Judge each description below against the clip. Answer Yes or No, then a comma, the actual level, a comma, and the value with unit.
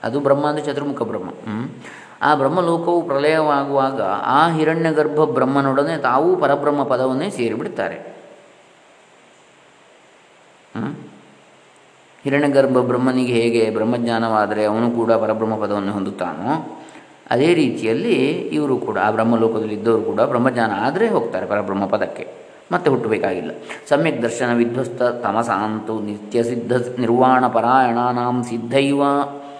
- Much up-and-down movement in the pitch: No, average, 3.8 semitones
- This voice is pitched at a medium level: No, low, 125 Hz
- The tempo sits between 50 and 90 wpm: No, average, 100 wpm